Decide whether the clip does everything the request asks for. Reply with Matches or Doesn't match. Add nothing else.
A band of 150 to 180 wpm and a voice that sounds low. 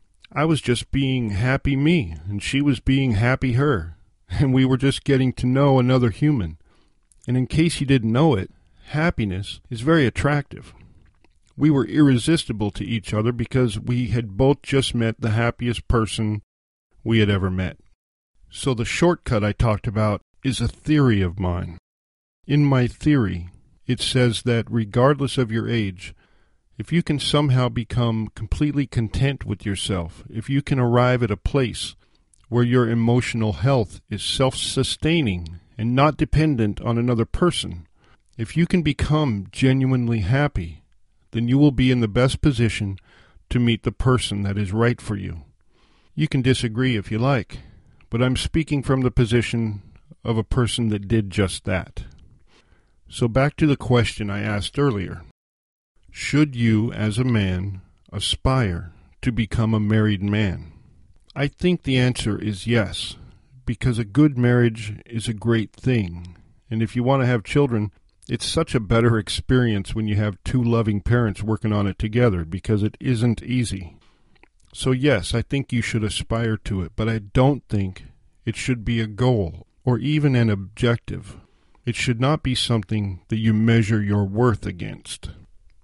Matches